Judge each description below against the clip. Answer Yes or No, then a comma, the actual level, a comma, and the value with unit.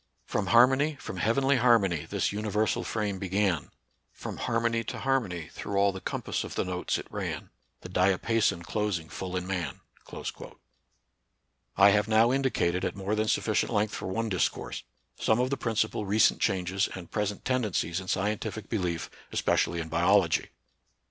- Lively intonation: No, average, 3.7 semitones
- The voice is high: No, low, 100 Hz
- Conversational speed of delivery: Yes, average, 160 wpm